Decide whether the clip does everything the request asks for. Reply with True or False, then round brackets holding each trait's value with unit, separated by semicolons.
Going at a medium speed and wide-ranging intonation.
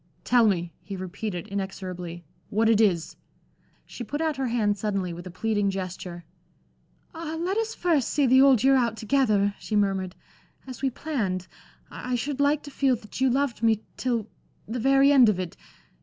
True (180 wpm; 5.7 semitones)